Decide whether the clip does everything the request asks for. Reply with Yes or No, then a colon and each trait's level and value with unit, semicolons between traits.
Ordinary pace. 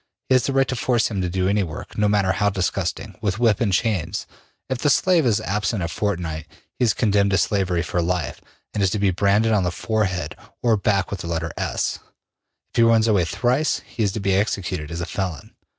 No: fast, 225 wpm